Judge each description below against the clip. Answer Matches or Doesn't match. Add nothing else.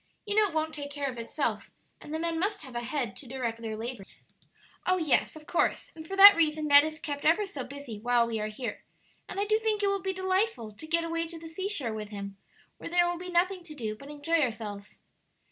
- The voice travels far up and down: Matches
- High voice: Matches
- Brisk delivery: Matches